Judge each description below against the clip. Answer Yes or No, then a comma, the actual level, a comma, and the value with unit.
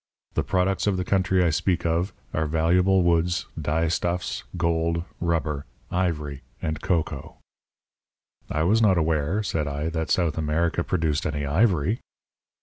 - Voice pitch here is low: Yes, very low, 85 Hz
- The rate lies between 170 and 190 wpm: No, average, 140 wpm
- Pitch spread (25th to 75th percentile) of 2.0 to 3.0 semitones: Yes, average, 2.7 semitones